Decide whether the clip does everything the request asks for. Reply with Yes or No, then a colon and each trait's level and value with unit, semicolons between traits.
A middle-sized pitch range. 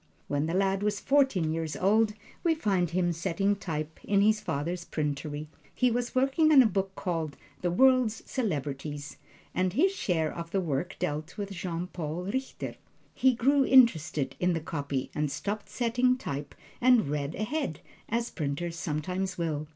No: wide, 6.5 semitones